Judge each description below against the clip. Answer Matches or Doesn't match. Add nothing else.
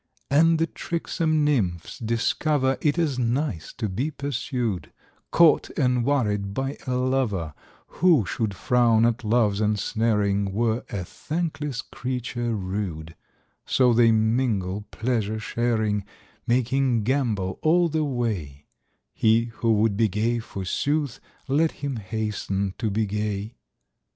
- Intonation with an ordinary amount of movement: Matches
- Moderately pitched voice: Doesn't match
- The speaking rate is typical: Doesn't match